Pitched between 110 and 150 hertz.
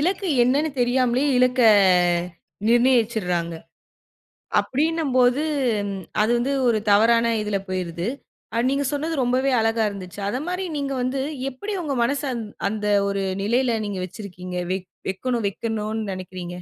No: high, 235 Hz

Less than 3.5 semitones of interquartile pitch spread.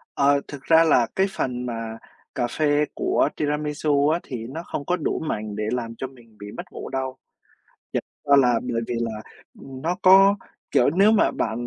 No: average, 4.3 semitones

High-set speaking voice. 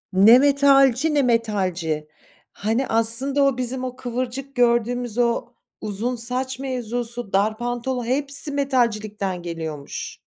Yes: high, 245 Hz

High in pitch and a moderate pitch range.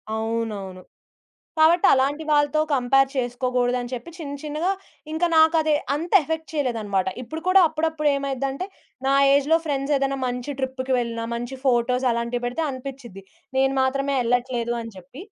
Yes: very high, 265 Hz; average, 3.4 semitones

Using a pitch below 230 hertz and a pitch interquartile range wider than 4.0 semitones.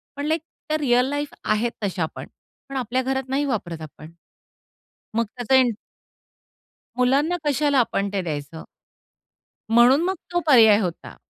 No: very high, 250 Hz; wide, 5.6 semitones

